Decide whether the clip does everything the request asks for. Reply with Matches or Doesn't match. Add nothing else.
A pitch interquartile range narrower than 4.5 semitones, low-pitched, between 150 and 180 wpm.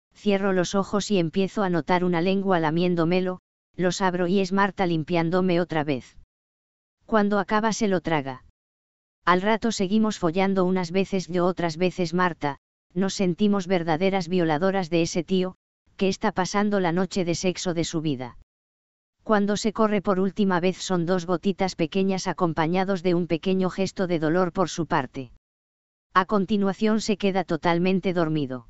Doesn't match